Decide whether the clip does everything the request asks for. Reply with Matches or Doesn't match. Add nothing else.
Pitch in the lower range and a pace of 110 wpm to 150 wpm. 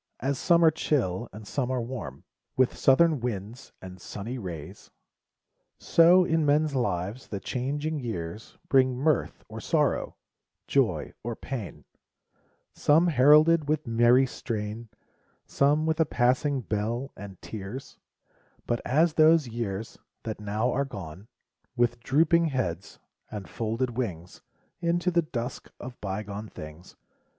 Matches